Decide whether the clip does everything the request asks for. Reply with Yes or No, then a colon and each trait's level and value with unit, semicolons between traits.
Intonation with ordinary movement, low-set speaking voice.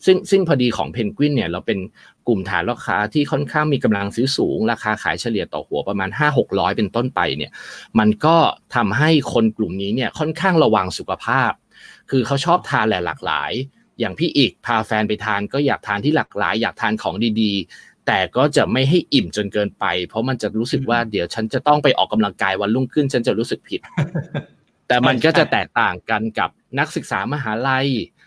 Yes: average, 4.7 semitones; low, 120 Hz